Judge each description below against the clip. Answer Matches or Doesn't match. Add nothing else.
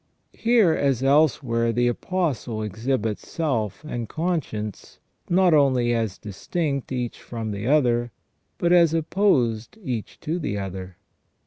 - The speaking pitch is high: Doesn't match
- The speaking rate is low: Matches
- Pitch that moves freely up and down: Matches